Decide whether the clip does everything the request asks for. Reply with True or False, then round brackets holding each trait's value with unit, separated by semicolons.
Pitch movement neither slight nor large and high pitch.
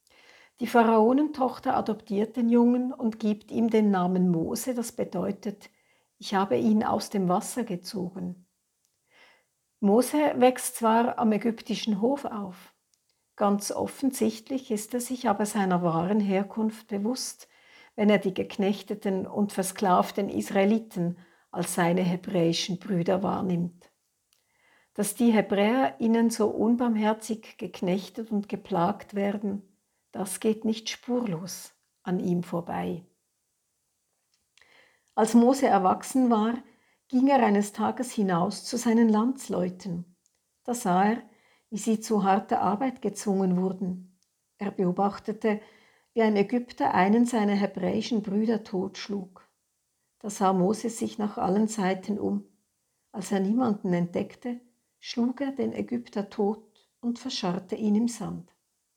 True (3.7 semitones; 210 Hz)